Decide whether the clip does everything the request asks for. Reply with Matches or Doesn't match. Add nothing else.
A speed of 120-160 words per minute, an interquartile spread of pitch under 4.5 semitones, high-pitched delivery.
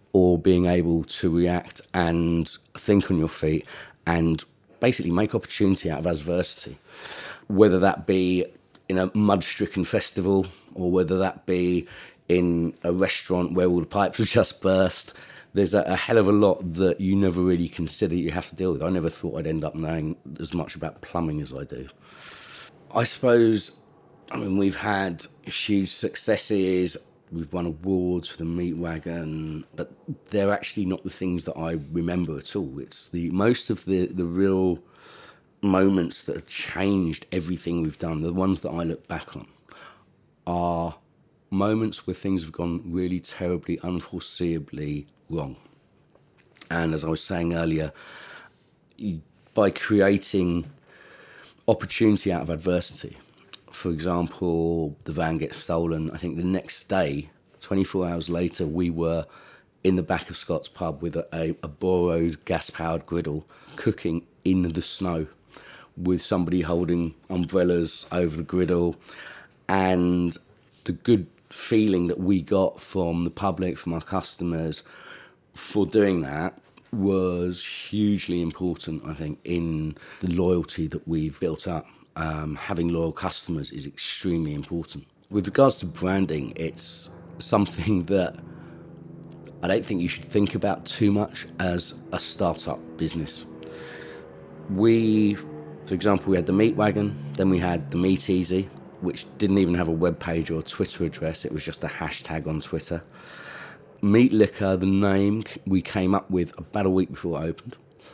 Doesn't match